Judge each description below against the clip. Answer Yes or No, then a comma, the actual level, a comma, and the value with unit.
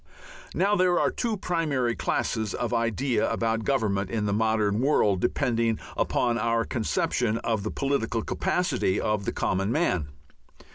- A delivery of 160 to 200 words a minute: No, average, 145 wpm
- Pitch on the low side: Yes, low, 115 Hz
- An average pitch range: Yes, average, 4.3 semitones